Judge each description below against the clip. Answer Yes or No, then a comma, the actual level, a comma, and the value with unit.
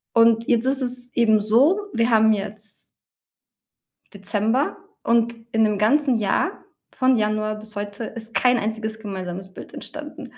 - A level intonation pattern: Yes, narrow, 2.3 semitones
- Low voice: No, high, 220 Hz